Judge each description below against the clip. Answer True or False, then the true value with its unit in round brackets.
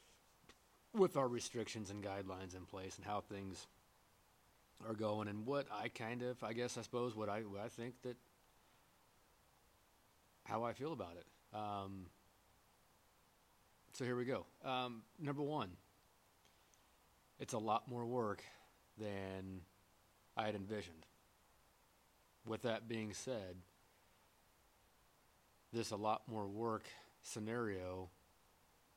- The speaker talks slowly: True (120 wpm)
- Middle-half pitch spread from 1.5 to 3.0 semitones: False (3.7 semitones)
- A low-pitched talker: True (105 Hz)